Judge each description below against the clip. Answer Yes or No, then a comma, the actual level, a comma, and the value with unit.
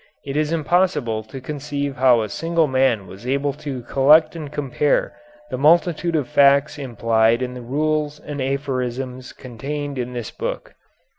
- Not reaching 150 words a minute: No, average, 155 wpm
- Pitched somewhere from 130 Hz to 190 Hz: Yes, medium, 140 Hz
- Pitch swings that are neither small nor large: Yes, average, 3.0 semitones